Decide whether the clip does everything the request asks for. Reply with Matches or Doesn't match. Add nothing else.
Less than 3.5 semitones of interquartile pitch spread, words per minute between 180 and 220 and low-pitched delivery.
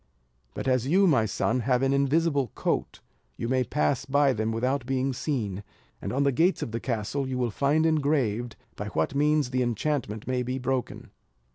Matches